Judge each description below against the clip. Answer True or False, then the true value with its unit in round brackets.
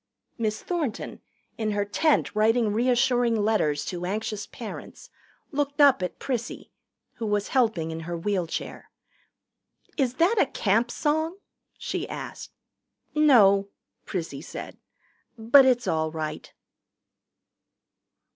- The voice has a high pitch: True (220 Hz)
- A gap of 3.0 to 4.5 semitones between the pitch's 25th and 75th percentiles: False (5.2 semitones)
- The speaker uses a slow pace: True (115 wpm)